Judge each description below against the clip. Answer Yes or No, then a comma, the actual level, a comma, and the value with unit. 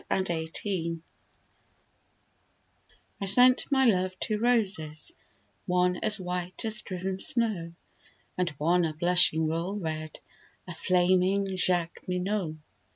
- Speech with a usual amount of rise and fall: Yes, average, 3.0 semitones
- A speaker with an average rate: No, slow, 110 wpm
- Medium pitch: Yes, medium, 180 Hz